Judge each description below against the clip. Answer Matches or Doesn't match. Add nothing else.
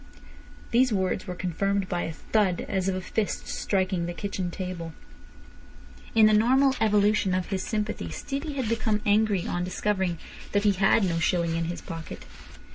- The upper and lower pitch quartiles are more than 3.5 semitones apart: Doesn't match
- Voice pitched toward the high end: Matches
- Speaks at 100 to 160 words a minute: Doesn't match